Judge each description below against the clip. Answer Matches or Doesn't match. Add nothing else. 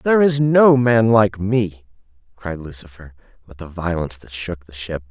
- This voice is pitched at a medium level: Doesn't match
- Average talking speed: Matches